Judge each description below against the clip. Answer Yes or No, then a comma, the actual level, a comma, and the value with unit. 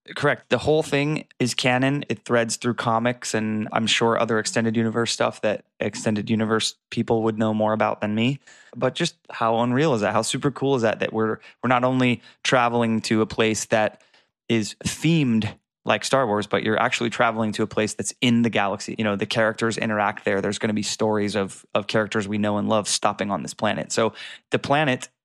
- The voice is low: Yes, low, 115 Hz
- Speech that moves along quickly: Yes, fast, 210 wpm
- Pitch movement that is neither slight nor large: No, narrow, 2.0 semitones